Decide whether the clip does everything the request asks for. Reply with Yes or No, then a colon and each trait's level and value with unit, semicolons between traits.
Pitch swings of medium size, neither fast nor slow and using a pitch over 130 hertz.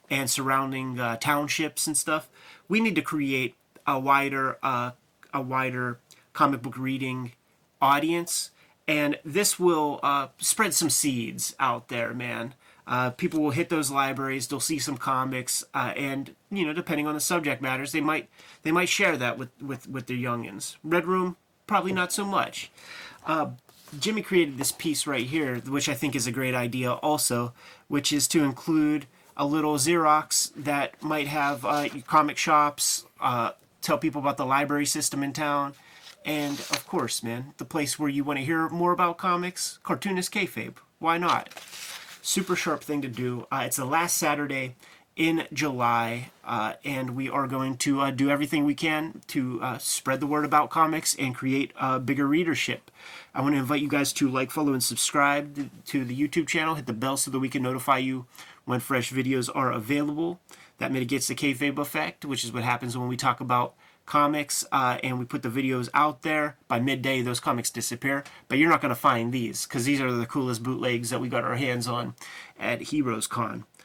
Yes: average, 3.0 semitones; average, 190 wpm; medium, 140 Hz